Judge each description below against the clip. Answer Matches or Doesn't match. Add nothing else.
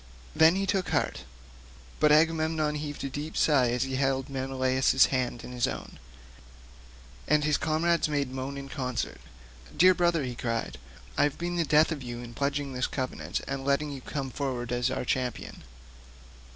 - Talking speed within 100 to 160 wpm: Doesn't match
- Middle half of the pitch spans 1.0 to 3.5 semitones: Matches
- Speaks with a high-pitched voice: Doesn't match